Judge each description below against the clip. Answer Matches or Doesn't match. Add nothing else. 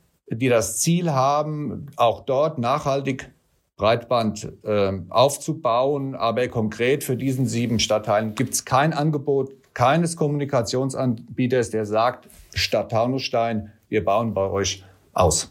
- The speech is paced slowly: Matches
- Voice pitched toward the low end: Matches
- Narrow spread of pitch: Doesn't match